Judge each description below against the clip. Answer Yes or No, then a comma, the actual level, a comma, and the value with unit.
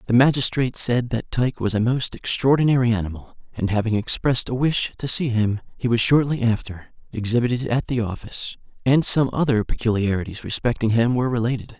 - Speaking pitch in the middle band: No, low, 120 Hz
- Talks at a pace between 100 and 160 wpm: No, average, 175 wpm